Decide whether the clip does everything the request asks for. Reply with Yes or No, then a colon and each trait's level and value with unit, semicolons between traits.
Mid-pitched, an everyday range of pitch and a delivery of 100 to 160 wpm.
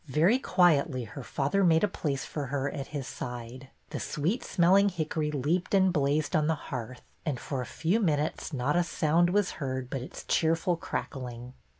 No: medium, 150 Hz; average, 4.5 semitones; average, 185 wpm